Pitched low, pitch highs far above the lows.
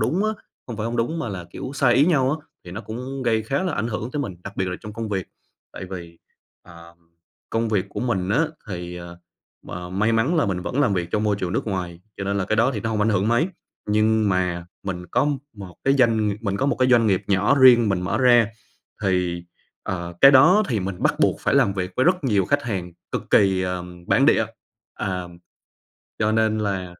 No: low, 105 Hz; average, 4.8 semitones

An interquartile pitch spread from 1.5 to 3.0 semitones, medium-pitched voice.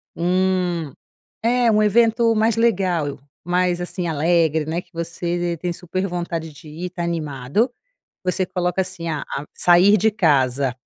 Yes: narrow, 2.6 semitones; medium, 175 Hz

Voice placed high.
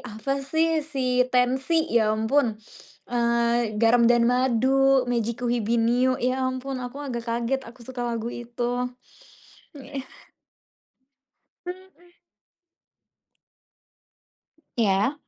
Yes: very high, 250 Hz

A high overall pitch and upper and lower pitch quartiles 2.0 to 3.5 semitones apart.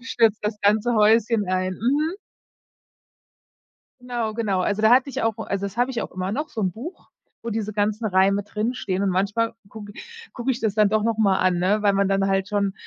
Yes: high, 210 Hz; narrow, 2.6 semitones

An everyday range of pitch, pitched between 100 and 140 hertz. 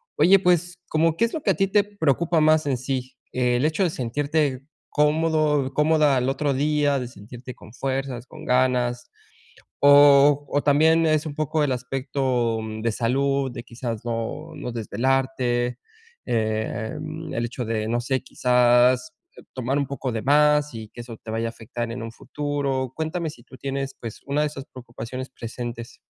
Yes: average, 3.5 semitones; low, 135 Hz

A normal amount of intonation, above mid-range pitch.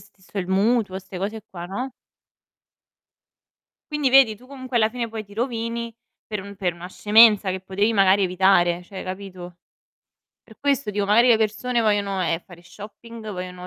Yes: average, 3.5 semitones; high, 205 Hz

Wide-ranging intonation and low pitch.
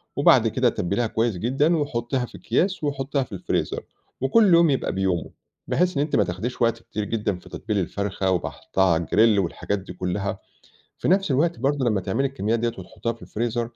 Yes: wide, 5.8 semitones; low, 115 Hz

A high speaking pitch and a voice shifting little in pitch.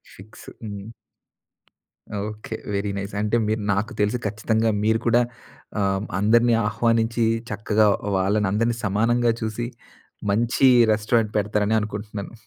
No: low, 110 Hz; narrow, 1.8 semitones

